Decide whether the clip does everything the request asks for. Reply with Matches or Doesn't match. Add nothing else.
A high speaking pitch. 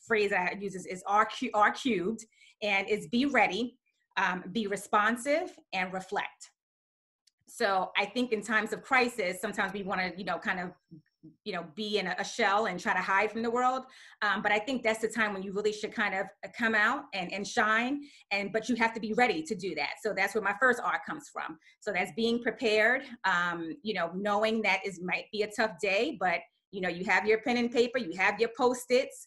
Matches